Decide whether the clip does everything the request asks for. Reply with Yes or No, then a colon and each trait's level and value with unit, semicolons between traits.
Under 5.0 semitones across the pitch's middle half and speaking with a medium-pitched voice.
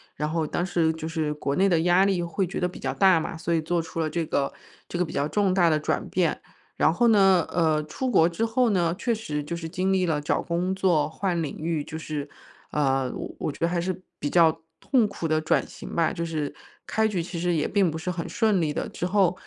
Yes: average, 3.0 semitones; medium, 170 Hz